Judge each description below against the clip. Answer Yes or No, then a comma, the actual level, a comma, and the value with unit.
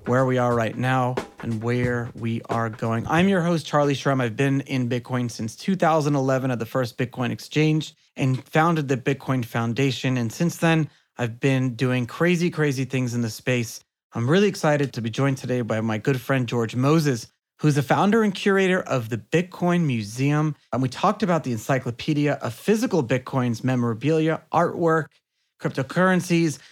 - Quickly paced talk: No, average, 175 wpm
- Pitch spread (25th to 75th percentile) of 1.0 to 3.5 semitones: No, average, 4.5 semitones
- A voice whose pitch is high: No, low, 135 Hz